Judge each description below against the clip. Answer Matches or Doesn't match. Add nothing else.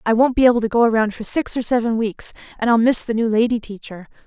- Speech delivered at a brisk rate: Matches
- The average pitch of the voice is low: Doesn't match